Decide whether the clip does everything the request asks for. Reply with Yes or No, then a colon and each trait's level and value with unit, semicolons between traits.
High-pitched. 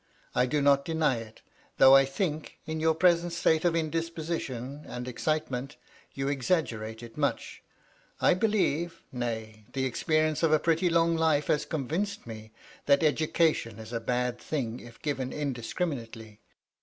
No: medium, 145 Hz